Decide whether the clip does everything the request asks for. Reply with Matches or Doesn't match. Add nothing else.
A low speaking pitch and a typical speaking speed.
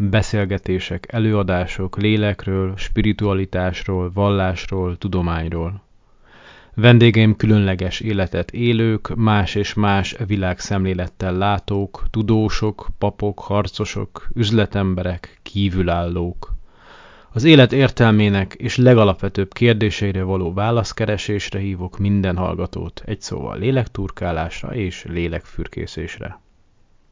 Doesn't match